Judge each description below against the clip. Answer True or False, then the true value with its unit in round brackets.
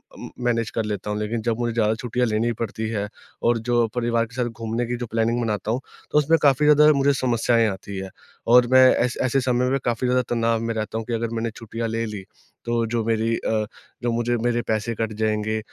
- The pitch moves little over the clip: True (1.5 semitones)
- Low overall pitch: True (115 Hz)